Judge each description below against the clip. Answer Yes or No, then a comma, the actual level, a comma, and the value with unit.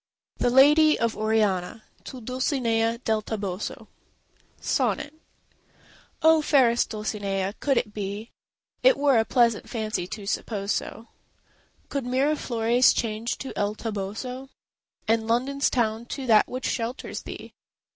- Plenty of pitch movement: No, average, 3.3 semitones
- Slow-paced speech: Yes, slow, 125 wpm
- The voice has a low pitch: No, high, 230 Hz